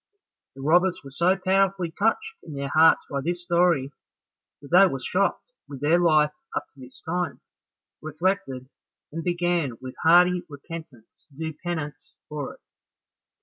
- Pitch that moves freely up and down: No, average, 3.8 semitones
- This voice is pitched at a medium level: Yes, medium, 165 Hz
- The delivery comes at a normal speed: Yes, average, 150 wpm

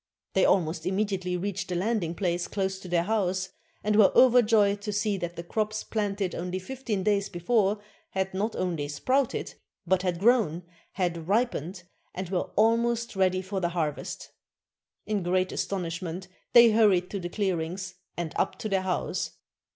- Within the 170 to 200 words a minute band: No, average, 160 wpm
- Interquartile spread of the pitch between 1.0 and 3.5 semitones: Yes, average, 3.0 semitones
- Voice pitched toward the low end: No, high, 190 Hz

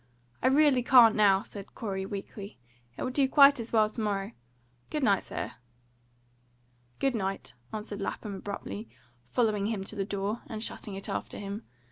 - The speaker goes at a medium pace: Yes, average, 165 wpm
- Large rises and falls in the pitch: No, average, 3.1 semitones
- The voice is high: Yes, high, 210 Hz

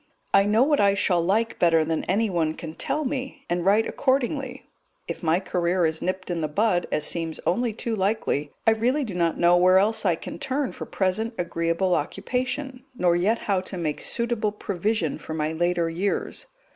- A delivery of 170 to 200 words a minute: Yes, average, 190 wpm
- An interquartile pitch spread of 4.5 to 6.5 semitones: Yes, average, 4.9 semitones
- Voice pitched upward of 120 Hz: Yes, high, 190 Hz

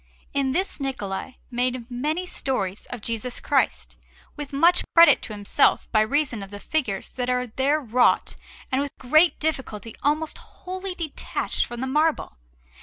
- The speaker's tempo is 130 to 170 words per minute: Yes, average, 155 wpm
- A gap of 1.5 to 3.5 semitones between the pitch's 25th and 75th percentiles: No, average, 4.8 semitones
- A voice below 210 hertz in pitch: No, very high, 265 Hz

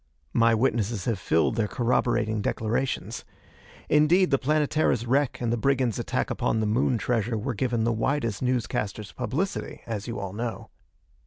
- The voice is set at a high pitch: No, low, 120 Hz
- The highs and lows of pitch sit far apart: No, average, 3.2 semitones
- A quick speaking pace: No, average, 160 wpm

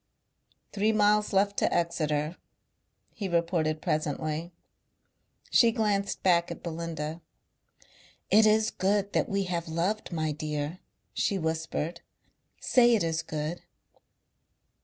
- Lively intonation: No, average, 4.3 semitones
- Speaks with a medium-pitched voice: Yes, medium, 170 Hz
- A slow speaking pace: Yes, slow, 115 wpm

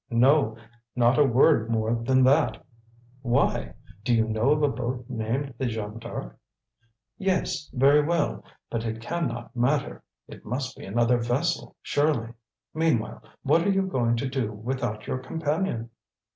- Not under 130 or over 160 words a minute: Yes, average, 155 wpm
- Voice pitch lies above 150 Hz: No, low, 125 Hz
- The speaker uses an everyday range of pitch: Yes, average, 4.0 semitones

